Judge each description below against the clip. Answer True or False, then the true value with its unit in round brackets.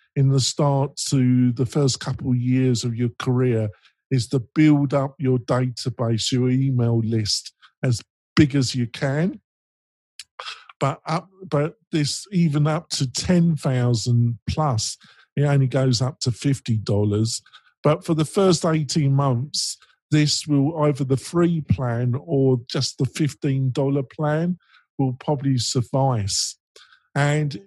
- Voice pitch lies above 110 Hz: True (135 Hz)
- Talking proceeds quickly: False (140 wpm)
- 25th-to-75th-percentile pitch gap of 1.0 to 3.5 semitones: True (3.2 semitones)